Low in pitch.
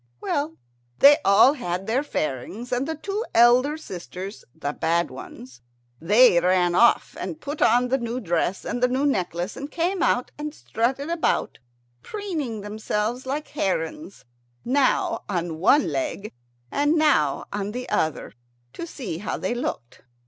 No: high, 240 Hz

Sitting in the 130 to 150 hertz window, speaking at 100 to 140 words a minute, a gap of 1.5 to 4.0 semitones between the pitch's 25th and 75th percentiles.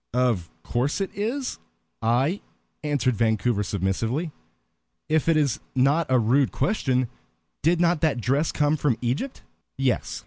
No: low, 135 Hz; slow, 135 wpm; average, 4.8 semitones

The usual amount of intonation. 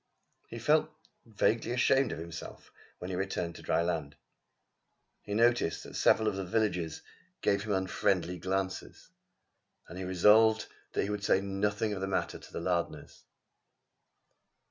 Yes: average, 3.4 semitones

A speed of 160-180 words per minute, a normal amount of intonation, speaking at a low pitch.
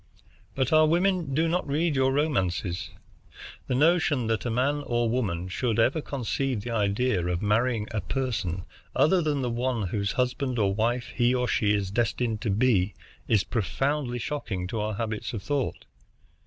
Yes: average, 170 wpm; average, 4.5 semitones; low, 120 Hz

